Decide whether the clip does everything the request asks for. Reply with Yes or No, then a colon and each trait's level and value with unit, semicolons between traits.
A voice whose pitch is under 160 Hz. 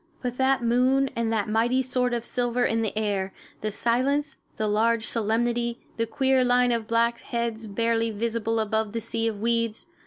No: high, 230 Hz